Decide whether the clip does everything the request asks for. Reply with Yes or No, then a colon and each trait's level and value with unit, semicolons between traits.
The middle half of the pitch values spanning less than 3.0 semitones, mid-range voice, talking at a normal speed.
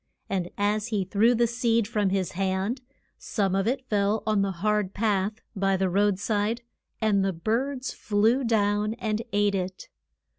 No: narrow, 2.4 semitones; high, 205 Hz; average, 170 wpm